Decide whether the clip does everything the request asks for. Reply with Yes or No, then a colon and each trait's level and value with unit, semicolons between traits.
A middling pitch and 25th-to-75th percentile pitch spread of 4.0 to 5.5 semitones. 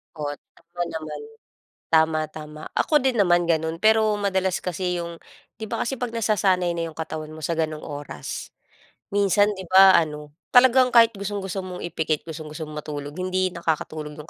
Yes: medium, 175 Hz; average, 4.3 semitones